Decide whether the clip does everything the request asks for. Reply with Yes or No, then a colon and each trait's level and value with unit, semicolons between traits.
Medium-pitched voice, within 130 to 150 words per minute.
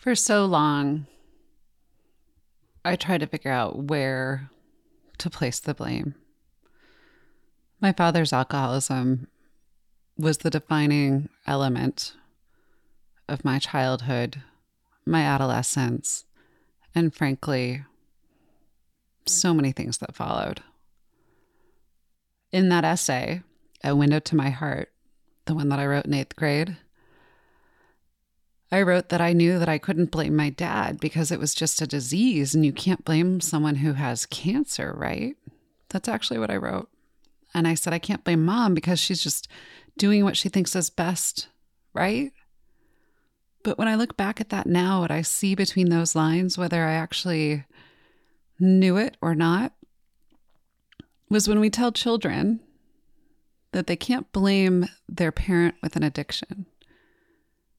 Yes: medium, 170 Hz; slow, 135 wpm